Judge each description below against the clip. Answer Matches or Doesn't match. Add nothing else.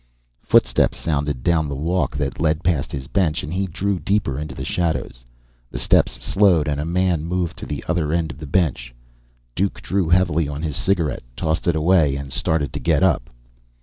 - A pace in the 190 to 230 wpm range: Matches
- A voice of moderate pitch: Doesn't match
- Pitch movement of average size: Matches